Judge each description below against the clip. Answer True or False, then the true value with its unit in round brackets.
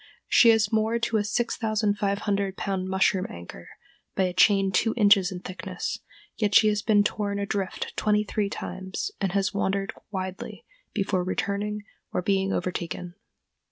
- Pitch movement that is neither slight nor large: False (1.8 semitones)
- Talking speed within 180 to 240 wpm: False (150 wpm)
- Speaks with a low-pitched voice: False (200 Hz)